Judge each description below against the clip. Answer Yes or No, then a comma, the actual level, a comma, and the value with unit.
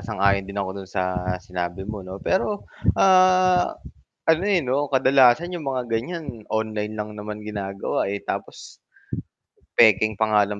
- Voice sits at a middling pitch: No, low, 110 Hz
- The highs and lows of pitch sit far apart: Yes, wide, 5.7 semitones